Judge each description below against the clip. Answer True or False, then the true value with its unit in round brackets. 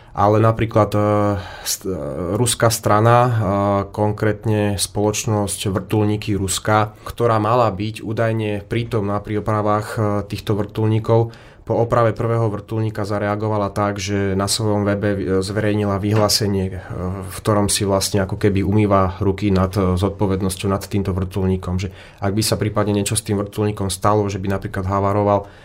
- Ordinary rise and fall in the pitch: False (1.5 semitones)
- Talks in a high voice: False (105 Hz)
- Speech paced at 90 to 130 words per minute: False (145 wpm)